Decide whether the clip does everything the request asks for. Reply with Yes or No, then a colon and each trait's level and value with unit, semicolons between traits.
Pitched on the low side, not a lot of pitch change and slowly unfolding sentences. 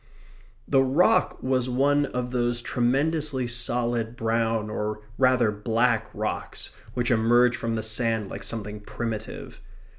Yes: low, 120 Hz; narrow, 2.2 semitones; slow, 125 wpm